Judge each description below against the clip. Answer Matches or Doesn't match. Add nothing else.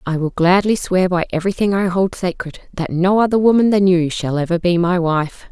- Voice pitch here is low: Doesn't match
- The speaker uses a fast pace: Matches